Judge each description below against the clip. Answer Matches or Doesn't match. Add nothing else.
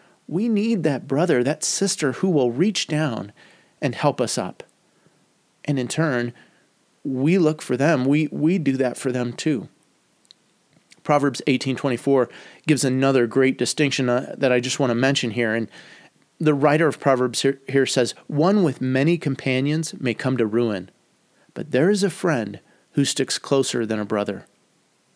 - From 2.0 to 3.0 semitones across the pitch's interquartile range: Doesn't match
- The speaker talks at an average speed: Matches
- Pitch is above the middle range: Doesn't match